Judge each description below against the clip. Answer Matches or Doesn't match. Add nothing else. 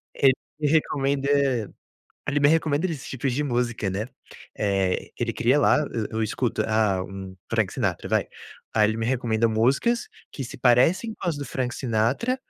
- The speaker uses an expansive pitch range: Doesn't match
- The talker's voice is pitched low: Matches